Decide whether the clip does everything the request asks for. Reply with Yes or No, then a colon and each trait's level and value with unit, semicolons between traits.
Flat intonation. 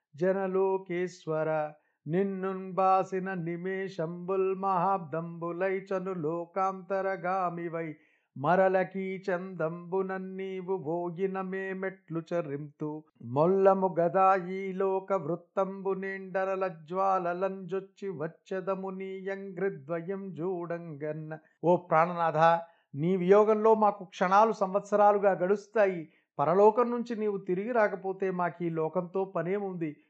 Yes: narrow, 2.1 semitones